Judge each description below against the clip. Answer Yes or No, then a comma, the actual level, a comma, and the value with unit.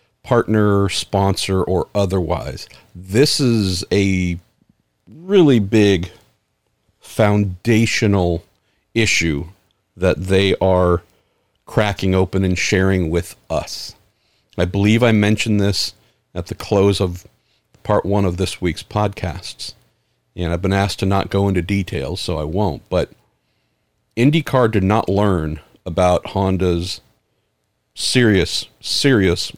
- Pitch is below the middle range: Yes, very low, 95 Hz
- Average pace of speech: No, slow, 115 wpm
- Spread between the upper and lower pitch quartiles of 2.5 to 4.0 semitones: Yes, average, 2.9 semitones